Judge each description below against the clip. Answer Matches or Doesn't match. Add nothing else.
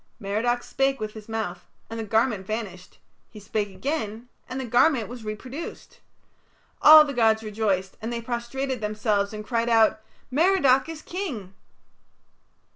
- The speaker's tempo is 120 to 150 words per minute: Matches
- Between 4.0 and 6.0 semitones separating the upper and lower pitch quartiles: Doesn't match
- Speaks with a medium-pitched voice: Doesn't match